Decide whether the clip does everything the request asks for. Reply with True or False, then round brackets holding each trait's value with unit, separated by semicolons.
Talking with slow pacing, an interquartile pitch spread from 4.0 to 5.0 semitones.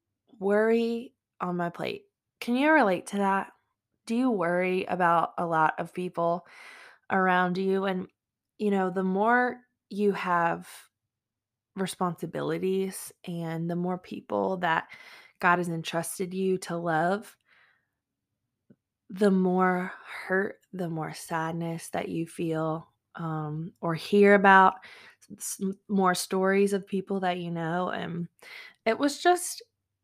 False (125 wpm; 3.3 semitones)